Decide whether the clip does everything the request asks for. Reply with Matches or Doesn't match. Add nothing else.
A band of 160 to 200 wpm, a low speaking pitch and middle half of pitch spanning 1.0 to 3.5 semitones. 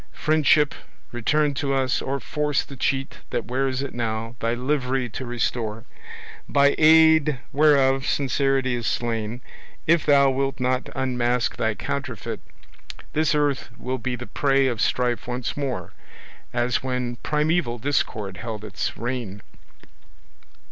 Doesn't match